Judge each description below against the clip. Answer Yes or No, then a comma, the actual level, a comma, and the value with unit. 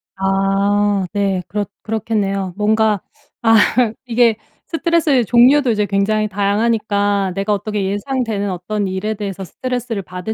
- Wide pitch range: No, narrow, 2.3 semitones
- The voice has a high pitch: Yes, high, 205 Hz